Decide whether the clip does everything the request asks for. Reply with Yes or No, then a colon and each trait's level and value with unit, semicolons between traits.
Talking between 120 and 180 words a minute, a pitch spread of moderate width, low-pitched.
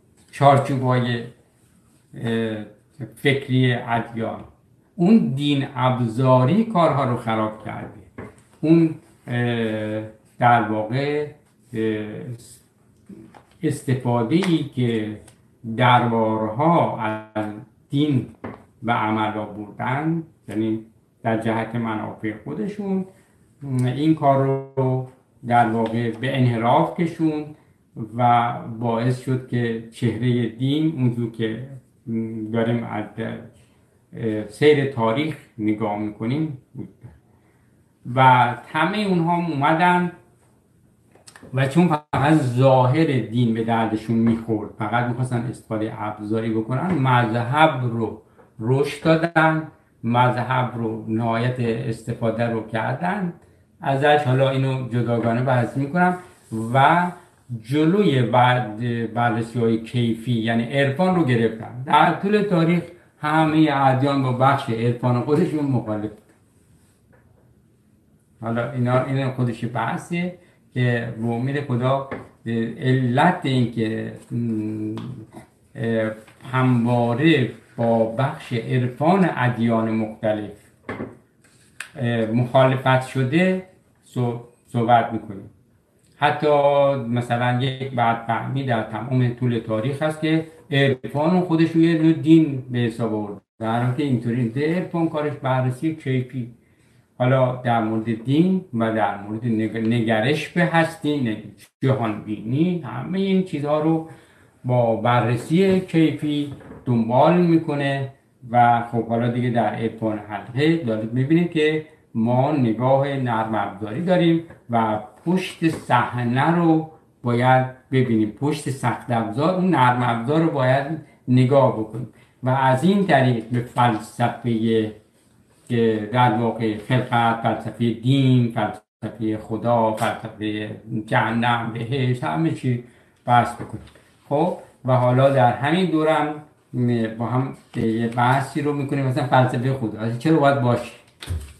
No: slow, 105 wpm; average, 3.9 semitones; low, 120 Hz